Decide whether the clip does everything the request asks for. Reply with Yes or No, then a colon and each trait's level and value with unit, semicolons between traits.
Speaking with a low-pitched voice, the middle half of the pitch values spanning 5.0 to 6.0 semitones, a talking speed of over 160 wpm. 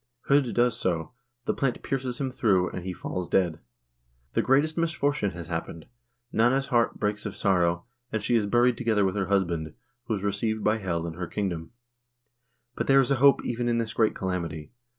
Yes: low, 105 Hz; wide, 5.4 semitones; average, 190 wpm